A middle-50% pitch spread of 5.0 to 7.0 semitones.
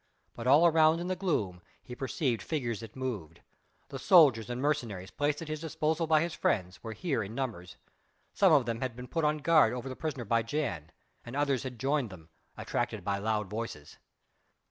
Yes: wide, 5.5 semitones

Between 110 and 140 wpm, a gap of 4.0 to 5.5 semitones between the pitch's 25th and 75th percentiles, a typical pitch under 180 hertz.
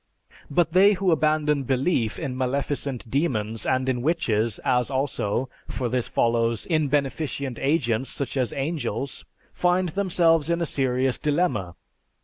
Yes: slow, 135 wpm; average, 4.5 semitones; low, 135 Hz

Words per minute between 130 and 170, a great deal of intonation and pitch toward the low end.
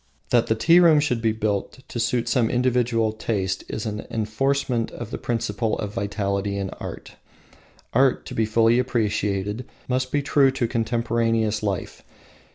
No: average, 160 wpm; average, 2.9 semitones; low, 115 Hz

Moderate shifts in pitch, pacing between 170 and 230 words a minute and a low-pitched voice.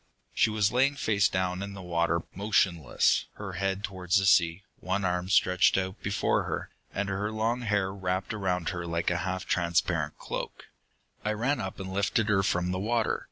No: narrow, 2.2 semitones; average, 185 wpm; very low, 95 Hz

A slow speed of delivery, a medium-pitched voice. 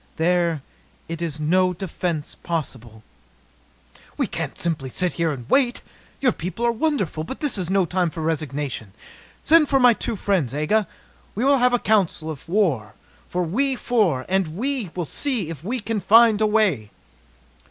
No: average, 155 wpm; medium, 180 Hz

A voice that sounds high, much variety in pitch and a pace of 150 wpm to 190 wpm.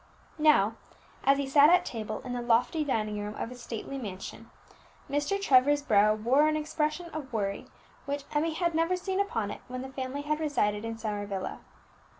Yes: very high, 265 Hz; wide, 5.8 semitones; average, 185 wpm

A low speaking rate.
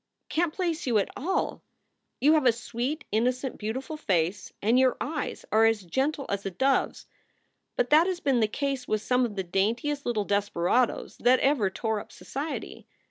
No: average, 190 wpm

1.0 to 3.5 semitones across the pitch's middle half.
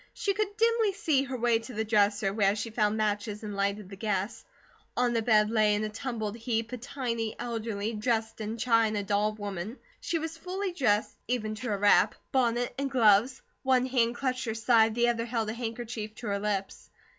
Yes: average, 2.9 semitones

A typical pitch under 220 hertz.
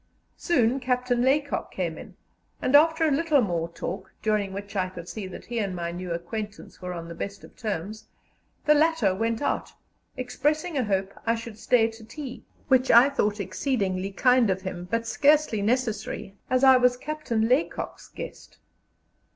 No: high, 225 Hz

